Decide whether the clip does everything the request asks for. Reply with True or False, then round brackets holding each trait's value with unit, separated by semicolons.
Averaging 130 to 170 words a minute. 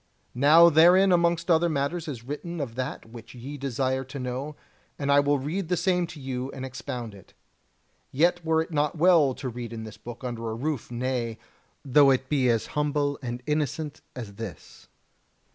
False (185 wpm)